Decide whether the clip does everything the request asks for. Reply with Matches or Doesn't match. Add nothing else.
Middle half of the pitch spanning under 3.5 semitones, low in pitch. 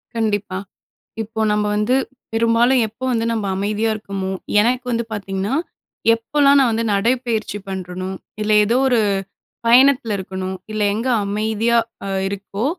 Doesn't match